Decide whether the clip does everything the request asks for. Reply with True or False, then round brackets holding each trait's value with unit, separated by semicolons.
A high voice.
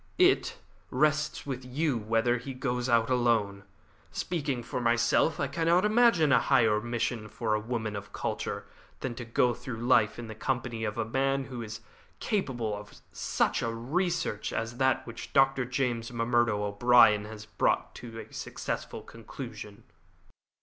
False (120 Hz)